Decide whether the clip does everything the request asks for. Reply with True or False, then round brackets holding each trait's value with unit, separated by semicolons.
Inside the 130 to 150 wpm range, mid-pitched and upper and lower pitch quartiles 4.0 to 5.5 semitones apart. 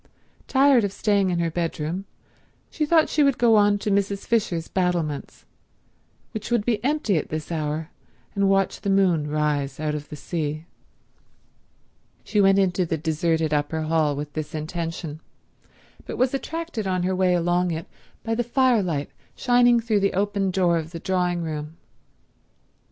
False (160 wpm; 180 Hz; 4.6 semitones)